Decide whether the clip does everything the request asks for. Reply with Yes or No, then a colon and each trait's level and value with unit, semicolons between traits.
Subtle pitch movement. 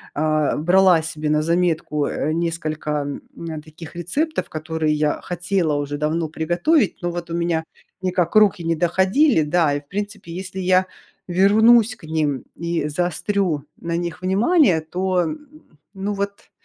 No: average, 3.4 semitones